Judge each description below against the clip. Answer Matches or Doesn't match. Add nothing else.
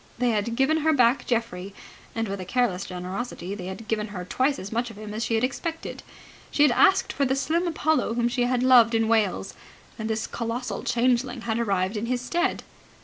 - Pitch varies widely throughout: Doesn't match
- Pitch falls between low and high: Doesn't match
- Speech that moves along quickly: Matches